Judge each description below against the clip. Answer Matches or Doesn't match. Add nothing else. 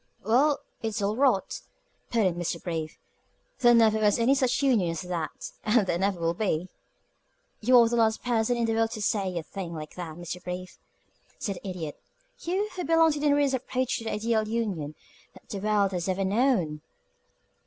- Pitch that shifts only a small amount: Doesn't match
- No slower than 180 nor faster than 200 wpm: Matches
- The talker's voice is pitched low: Doesn't match